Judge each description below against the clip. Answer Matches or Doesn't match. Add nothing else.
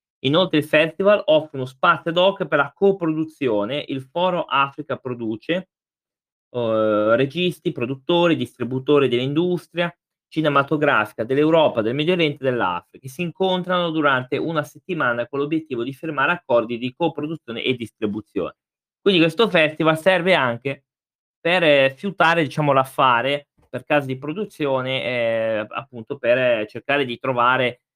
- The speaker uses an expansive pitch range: Doesn't match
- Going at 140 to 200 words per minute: Doesn't match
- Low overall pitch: Doesn't match